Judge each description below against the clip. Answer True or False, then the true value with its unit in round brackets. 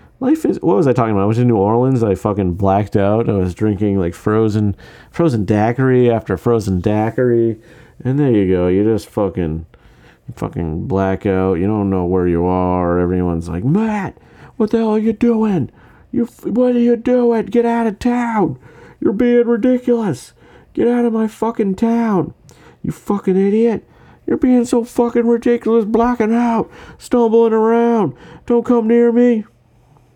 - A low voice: False (150 Hz)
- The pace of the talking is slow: False (170 wpm)